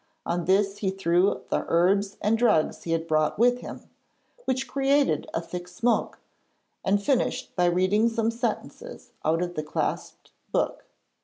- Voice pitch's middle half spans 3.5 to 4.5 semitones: No, average, 5.0 semitones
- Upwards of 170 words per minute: No, average, 155 wpm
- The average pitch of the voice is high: Yes, high, 195 Hz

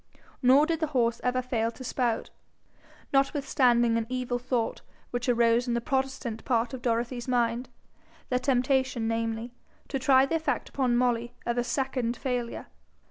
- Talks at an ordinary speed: Yes, average, 155 wpm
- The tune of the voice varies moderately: No, narrow, 1.9 semitones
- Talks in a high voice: Yes, high, 245 Hz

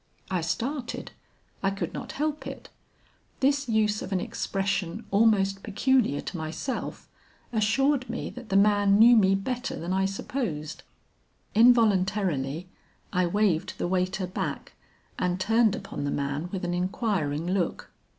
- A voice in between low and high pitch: No, high, 195 Hz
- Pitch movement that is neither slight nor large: Yes, average, 4.1 semitones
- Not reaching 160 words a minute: Yes, average, 140 wpm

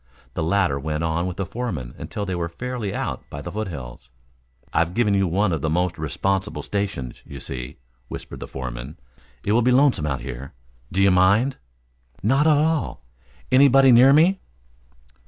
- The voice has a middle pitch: No, very low, 95 Hz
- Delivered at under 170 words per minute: No, average, 175 wpm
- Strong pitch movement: Yes, wide, 7.8 semitones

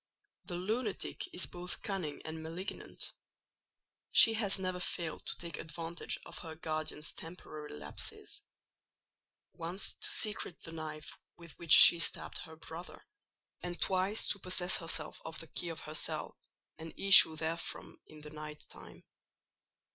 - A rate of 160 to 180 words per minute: No, average, 145 wpm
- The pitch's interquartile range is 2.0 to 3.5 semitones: Yes, narrow, 2.5 semitones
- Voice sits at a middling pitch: Yes, medium, 165 Hz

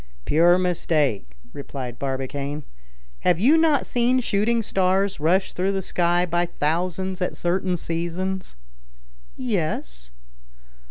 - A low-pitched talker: No, medium, 175 Hz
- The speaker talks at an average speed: No, slow, 110 wpm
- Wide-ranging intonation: No, average, 4.2 semitones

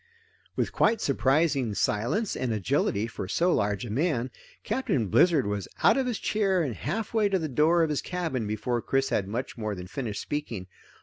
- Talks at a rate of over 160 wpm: Yes, average, 190 wpm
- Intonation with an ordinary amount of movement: No, wide, 8.1 semitones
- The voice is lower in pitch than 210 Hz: Yes, low, 135 Hz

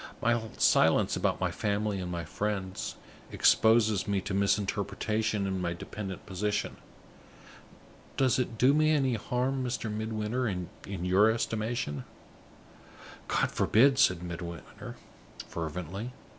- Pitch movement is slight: No, average, 3.9 semitones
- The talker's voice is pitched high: No, low, 105 Hz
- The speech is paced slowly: Yes, slow, 115 wpm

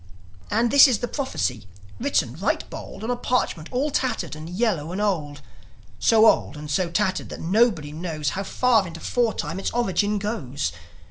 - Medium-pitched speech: No, high, 195 Hz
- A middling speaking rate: Yes, average, 175 wpm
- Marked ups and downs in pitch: Yes, wide, 6.9 semitones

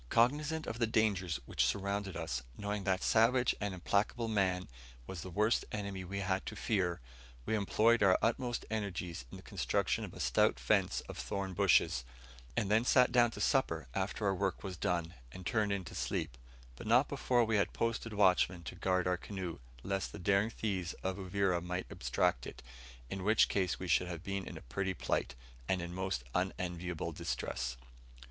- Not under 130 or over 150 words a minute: No, average, 185 wpm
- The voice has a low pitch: Yes, very low, 95 Hz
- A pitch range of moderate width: Yes, average, 3.2 semitones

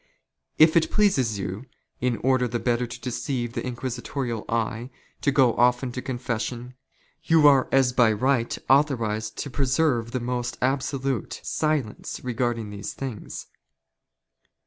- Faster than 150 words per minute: No, average, 145 wpm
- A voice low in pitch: Yes, low, 125 Hz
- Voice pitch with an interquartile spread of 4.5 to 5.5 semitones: No, narrow, 2.4 semitones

